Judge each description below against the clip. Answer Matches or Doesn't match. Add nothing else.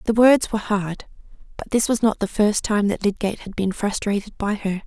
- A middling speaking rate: Doesn't match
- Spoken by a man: Doesn't match